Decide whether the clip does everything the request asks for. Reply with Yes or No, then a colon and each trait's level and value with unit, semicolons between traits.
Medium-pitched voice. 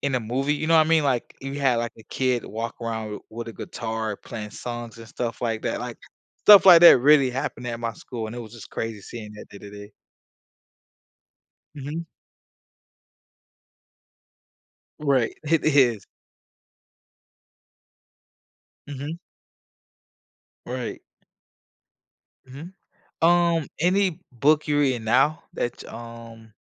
No: low, 125 Hz